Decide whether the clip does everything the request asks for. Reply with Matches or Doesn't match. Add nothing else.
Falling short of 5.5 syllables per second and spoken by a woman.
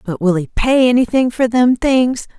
Matches